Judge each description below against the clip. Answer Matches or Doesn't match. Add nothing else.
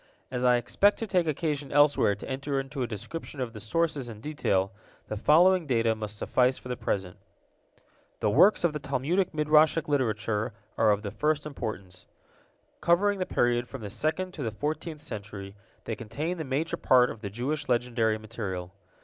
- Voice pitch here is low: Matches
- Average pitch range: Doesn't match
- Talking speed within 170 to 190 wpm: Matches